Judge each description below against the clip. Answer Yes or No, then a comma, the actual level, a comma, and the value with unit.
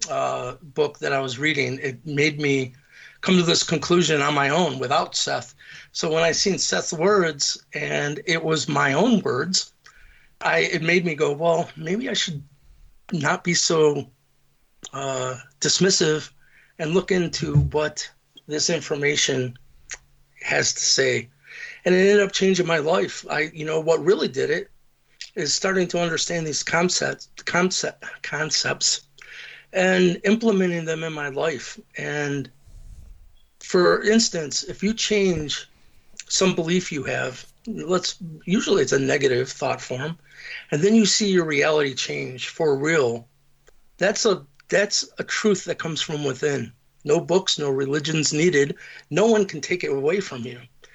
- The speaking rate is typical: Yes, average, 155 wpm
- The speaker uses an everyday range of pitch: Yes, average, 4.4 semitones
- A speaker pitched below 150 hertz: No, medium, 160 Hz